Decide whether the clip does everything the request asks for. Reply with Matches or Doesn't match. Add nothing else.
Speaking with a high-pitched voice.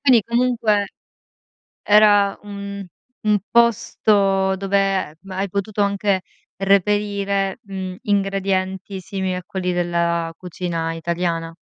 Matches